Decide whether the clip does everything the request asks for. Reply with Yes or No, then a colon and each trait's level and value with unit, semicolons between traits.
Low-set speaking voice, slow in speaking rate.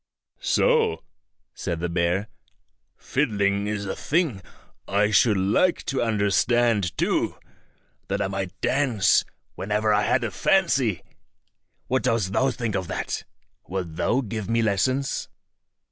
Yes: low, 105 Hz; slow, 130 wpm